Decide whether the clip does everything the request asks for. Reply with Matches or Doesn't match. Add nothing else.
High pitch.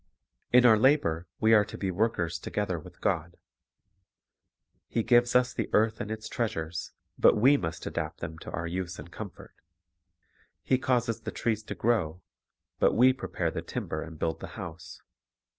Doesn't match